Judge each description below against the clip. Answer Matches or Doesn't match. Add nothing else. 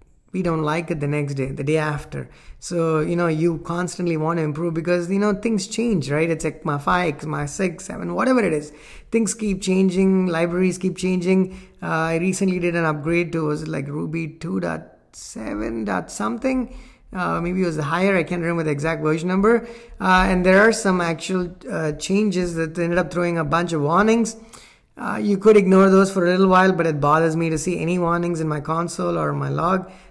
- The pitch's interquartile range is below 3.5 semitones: Matches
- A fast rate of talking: Matches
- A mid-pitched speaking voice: Matches